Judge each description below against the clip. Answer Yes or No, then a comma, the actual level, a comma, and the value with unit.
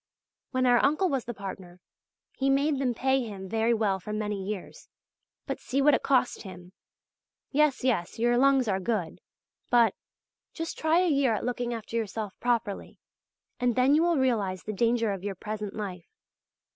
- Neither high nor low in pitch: No, high, 235 Hz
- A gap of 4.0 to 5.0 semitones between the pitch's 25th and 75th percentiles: Yes, average, 4.6 semitones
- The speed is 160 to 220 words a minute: Yes, average, 175 wpm